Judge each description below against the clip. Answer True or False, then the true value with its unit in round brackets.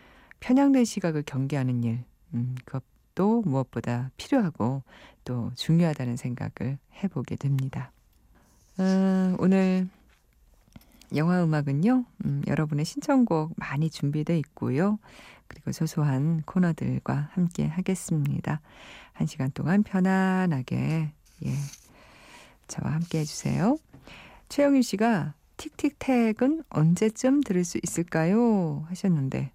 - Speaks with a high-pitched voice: False (160 Hz)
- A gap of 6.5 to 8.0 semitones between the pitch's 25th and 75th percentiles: False (6.0 semitones)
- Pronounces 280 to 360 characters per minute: False (250 characters per minute)